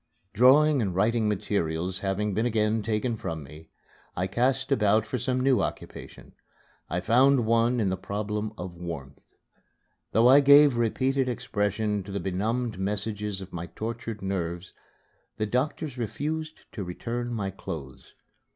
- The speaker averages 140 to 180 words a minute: Yes, average, 145 wpm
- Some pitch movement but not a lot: Yes, average, 4.2 semitones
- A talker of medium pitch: No, low, 105 Hz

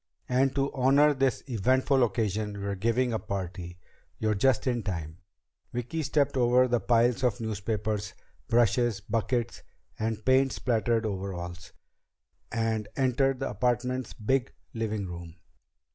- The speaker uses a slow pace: Yes, slow, 130 wpm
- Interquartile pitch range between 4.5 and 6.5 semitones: No, average, 3.6 semitones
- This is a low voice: Yes, low, 115 Hz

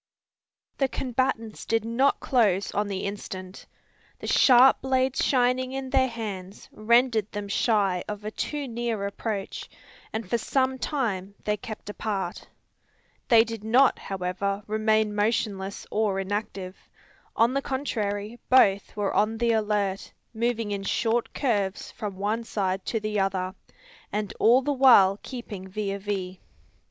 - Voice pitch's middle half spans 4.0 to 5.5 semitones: No, average, 3.2 semitones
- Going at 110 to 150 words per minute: Yes, average, 145 wpm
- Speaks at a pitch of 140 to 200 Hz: No, high, 215 Hz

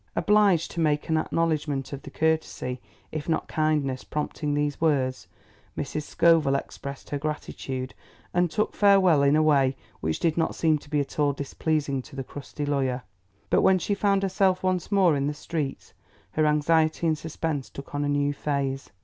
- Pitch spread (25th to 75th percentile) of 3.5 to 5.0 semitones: No, average, 2.8 semitones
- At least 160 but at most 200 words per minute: Yes, average, 175 wpm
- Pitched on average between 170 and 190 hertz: No, medium, 150 Hz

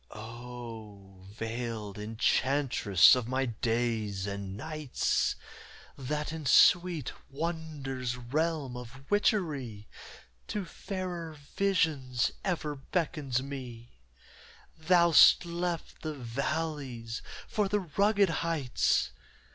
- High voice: No, low, 135 Hz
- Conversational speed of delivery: No, slow, 90 wpm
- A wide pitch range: Yes, wide, 5.7 semitones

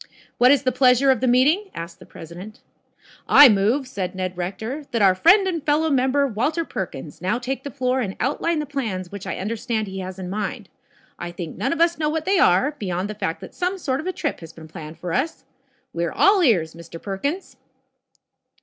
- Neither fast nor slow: No, fast, 215 wpm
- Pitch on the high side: Yes, high, 235 Hz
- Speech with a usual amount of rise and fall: No, wide, 7.6 semitones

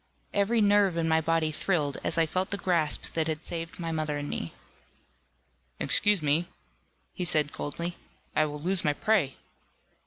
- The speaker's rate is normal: Yes, average, 165 wpm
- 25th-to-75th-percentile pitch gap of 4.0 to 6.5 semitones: No, average, 3.2 semitones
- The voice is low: No, medium, 165 Hz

